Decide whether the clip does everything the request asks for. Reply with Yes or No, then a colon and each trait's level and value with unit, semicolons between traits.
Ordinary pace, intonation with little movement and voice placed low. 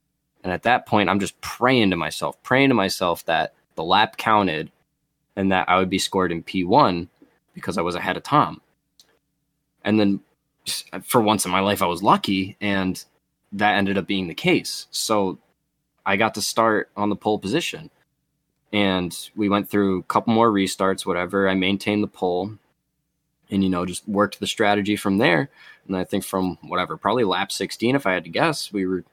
Yes: average, 190 wpm; narrow, 2.0 semitones; very low, 95 Hz